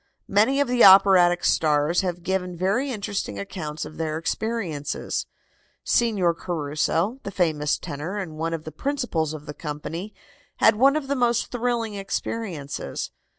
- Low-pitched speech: No, medium, 180 Hz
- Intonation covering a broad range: Yes, wide, 6.2 semitones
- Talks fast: No, average, 150 wpm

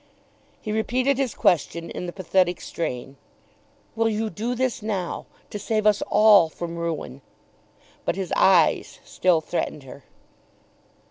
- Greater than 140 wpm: No, slow, 135 wpm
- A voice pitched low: No, high, 190 Hz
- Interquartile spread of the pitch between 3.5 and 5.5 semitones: Yes, average, 4.6 semitones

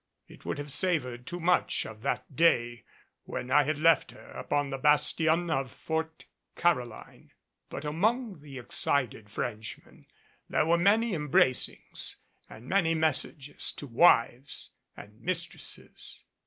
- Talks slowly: Yes, slow, 130 wpm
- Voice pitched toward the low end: No, medium, 150 Hz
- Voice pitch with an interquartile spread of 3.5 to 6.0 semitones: Yes, average, 4.8 semitones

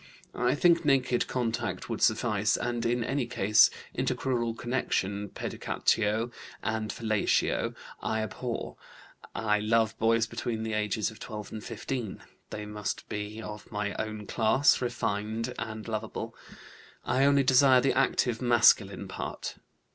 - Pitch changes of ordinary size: No, narrow, 2.3 semitones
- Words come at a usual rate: No, slow, 130 wpm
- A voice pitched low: Yes, low, 115 Hz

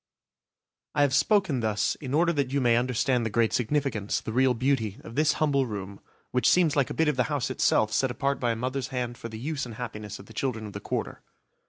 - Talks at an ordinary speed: No, fast, 235 wpm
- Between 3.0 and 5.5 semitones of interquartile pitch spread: Yes, average, 3.9 semitones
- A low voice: Yes, low, 125 Hz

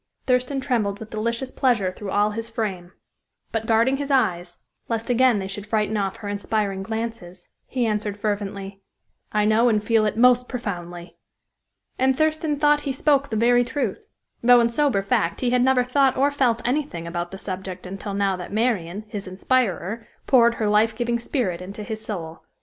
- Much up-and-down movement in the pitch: No, average, 4.1 semitones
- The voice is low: No, high, 220 Hz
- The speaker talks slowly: No, average, 180 wpm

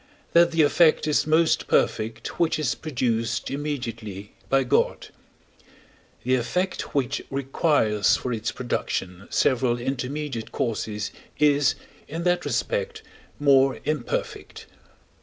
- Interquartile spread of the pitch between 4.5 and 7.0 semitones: Yes, average, 5.0 semitones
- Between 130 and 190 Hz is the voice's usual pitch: Yes, low, 135 Hz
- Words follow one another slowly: Yes, slow, 110 wpm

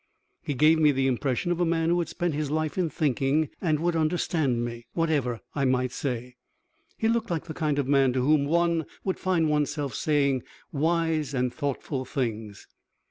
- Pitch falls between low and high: Yes, medium, 150 Hz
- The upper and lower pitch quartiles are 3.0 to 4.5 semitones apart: Yes, average, 3.7 semitones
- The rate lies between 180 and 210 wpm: Yes, average, 190 wpm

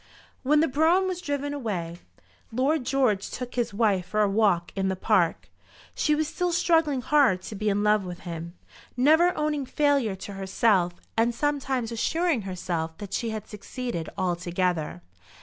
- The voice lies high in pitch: Yes, high, 225 Hz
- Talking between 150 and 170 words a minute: Yes, average, 165 wpm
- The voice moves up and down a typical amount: No, wide, 7.2 semitones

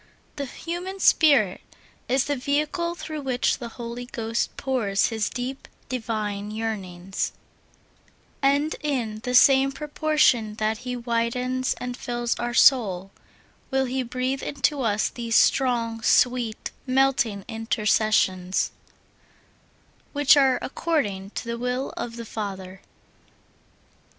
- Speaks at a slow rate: Yes, slow, 120 wpm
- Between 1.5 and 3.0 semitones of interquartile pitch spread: No, average, 3.6 semitones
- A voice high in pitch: Yes, high, 245 Hz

